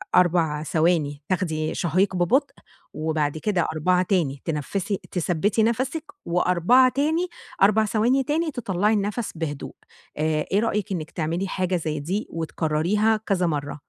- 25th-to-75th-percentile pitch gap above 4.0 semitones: Yes, average, 5.1 semitones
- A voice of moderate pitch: Yes, medium, 180 Hz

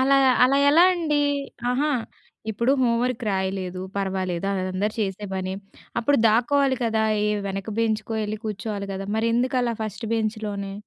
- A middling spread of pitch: Yes, average, 3.9 semitones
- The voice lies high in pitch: Yes, high, 215 Hz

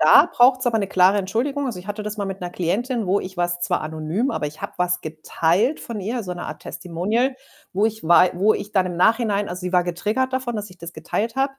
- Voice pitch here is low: No, high, 195 Hz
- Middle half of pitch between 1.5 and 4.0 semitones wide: No, average, 4.5 semitones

